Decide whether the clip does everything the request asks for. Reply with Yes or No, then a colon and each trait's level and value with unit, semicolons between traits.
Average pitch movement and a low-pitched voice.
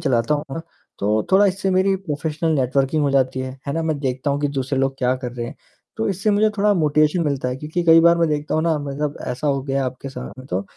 No: average, 3.8 semitones; medium, 145 Hz